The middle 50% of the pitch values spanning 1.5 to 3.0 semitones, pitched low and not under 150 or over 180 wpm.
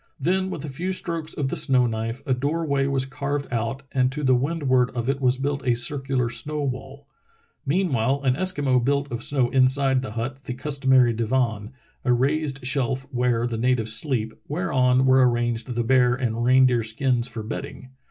No: narrow, 2.4 semitones; low, 130 Hz; average, 190 wpm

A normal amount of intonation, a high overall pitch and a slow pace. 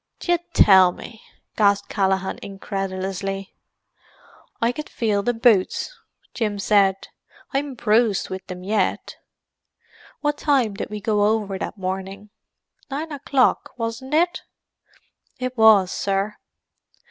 Yes: average, 3.9 semitones; high, 210 Hz; slow, 110 wpm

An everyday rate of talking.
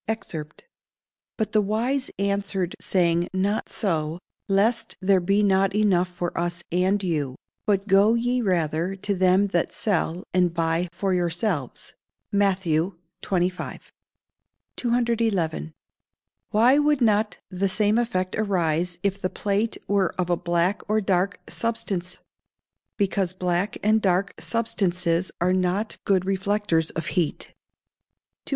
No: slow, 130 wpm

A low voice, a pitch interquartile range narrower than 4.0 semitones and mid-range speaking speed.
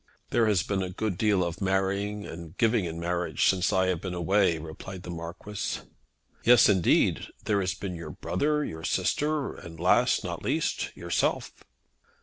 Yes: very low, 95 Hz; average, 3.3 semitones; average, 165 wpm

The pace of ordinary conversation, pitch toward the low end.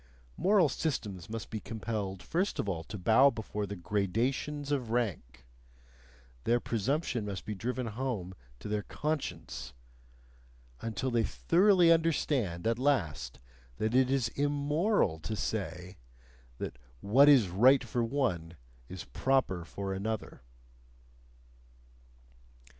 No: slow, 120 wpm; low, 115 Hz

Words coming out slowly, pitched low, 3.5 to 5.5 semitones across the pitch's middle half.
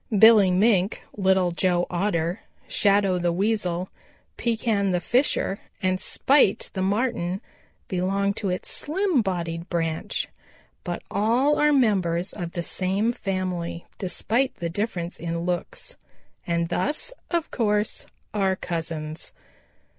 No: slow, 120 wpm; high, 190 Hz; average, 3.9 semitones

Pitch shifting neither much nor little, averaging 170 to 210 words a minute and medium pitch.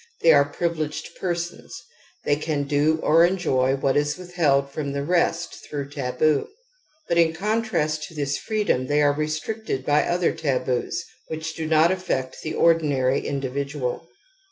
No: average, 3.1 semitones; average, 155 wpm; medium, 150 Hz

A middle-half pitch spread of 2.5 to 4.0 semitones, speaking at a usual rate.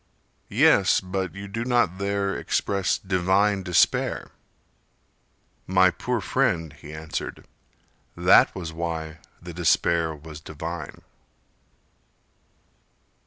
No: average, 3.3 semitones; slow, 95 wpm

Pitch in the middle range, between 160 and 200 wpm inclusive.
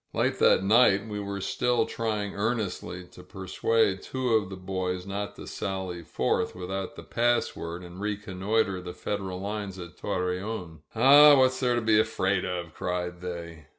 No: very low, 95 Hz; average, 165 wpm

